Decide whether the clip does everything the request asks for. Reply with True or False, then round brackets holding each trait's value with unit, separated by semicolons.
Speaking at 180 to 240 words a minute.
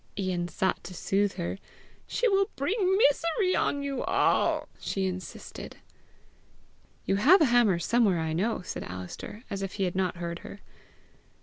False (160 wpm)